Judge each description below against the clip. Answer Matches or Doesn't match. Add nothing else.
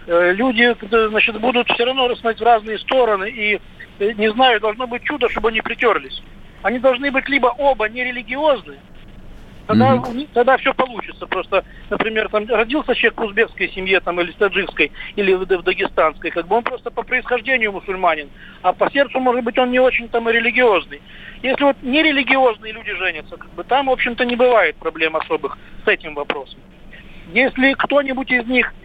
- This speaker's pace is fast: Matches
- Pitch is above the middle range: Matches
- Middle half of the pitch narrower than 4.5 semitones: Matches